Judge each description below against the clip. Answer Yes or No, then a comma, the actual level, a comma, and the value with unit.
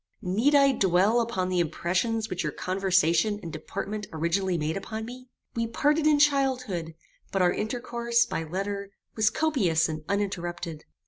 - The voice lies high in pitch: Yes, high, 200 Hz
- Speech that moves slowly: No, average, 150 wpm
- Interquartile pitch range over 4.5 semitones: Yes, average, 5.3 semitones